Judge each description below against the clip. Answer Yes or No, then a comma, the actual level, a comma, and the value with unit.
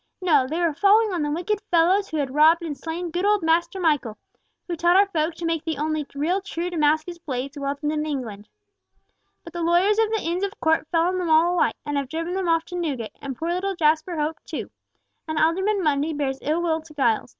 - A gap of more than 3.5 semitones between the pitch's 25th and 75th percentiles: No, average, 2.9 semitones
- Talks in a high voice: Yes, very high, 325 Hz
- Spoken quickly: Yes, fast, 230 wpm